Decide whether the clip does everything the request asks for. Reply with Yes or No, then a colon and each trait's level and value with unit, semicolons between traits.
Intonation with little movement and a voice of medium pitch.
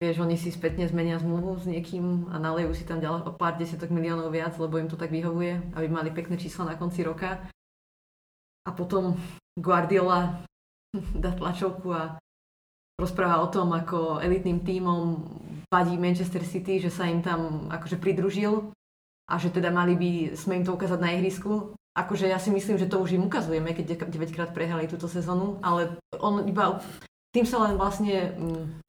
Yes: narrow, 1.8 semitones; medium, 175 Hz